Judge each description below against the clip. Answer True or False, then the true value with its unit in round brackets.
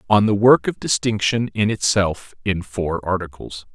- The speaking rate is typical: True (160 wpm)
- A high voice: False (100 Hz)